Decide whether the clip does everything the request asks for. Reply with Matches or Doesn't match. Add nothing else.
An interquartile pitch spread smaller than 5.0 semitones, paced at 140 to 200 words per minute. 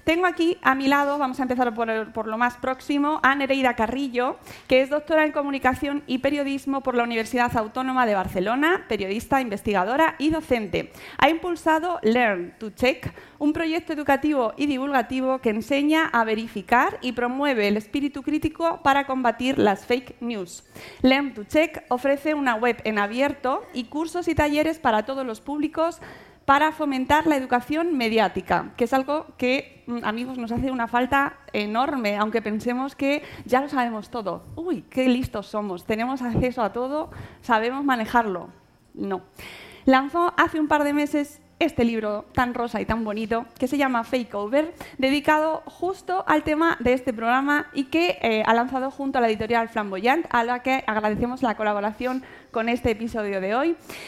Matches